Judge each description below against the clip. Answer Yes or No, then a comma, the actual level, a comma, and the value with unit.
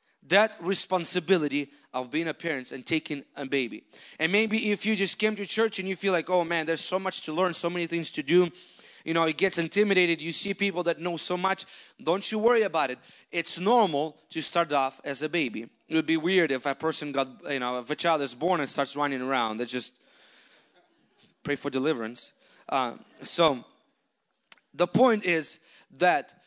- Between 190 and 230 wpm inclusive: Yes, average, 200 wpm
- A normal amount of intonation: Yes, average, 4.4 semitones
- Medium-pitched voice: Yes, medium, 170 Hz